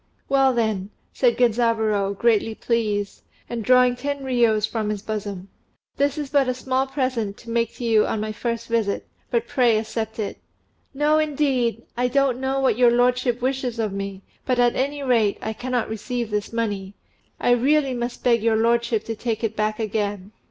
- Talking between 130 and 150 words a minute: No, average, 180 wpm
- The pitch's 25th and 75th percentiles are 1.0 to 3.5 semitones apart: Yes, average, 2.9 semitones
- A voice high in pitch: Yes, high, 235 Hz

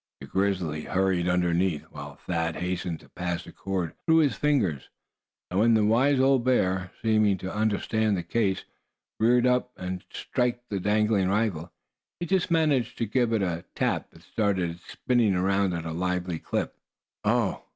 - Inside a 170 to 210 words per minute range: Yes, average, 175 wpm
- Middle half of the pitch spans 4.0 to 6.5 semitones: Yes, average, 4.7 semitones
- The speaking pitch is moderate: No, very low, 95 Hz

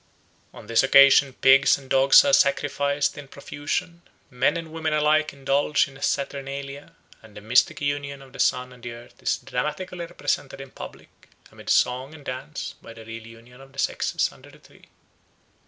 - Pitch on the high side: No, medium, 140 Hz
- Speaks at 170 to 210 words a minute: Yes, average, 180 wpm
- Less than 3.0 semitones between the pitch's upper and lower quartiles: Yes, narrow, 2.4 semitones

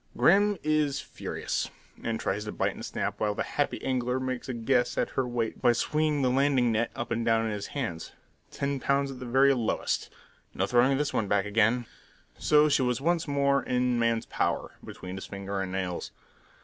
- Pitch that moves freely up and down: No, average, 3.7 semitones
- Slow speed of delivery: No, average, 200 wpm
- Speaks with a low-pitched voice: Yes, low, 125 Hz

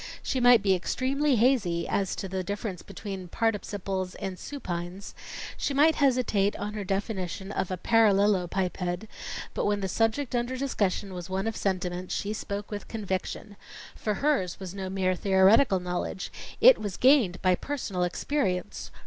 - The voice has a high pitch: Yes, high, 200 Hz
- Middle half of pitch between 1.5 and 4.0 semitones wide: Yes, average, 3.5 semitones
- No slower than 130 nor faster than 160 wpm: Yes, average, 155 wpm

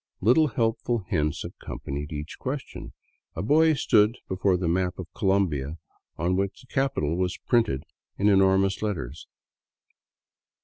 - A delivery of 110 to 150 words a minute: Yes, slow, 135 wpm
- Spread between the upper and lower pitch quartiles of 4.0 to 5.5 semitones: Yes, average, 5.2 semitones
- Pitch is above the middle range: No, very low, 95 Hz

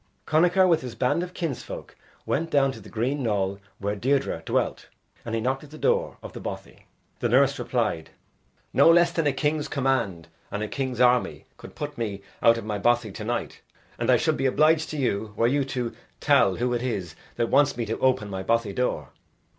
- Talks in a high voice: No, low, 125 Hz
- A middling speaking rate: No, fast, 210 wpm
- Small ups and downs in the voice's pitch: No, average, 4.9 semitones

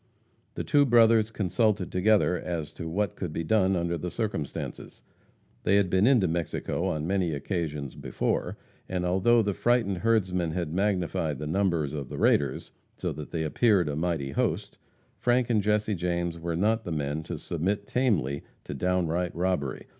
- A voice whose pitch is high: No, very low, 90 Hz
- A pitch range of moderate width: Yes, average, 4.3 semitones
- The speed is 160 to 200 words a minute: Yes, average, 170 wpm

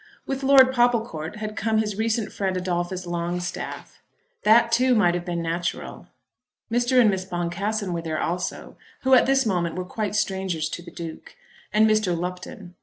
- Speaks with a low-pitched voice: No, high, 190 Hz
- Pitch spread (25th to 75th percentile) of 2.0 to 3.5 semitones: No, average, 4.3 semitones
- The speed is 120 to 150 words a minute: No, average, 170 wpm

